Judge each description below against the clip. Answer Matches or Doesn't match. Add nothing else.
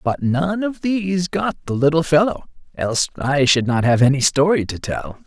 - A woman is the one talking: Doesn't match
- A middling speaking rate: Matches